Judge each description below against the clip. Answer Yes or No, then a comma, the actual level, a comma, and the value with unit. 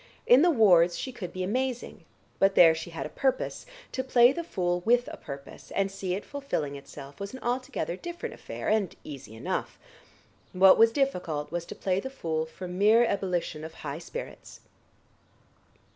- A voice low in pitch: No, high, 190 Hz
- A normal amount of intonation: No, wide, 6.7 semitones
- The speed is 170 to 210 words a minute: Yes, average, 180 wpm